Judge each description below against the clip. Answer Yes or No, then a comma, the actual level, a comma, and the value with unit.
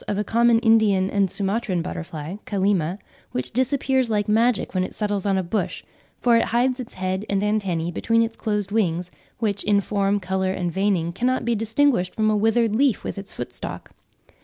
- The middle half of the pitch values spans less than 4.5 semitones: Yes, average, 3.2 semitones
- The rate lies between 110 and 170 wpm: No, average, 185 wpm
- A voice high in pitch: Yes, high, 205 Hz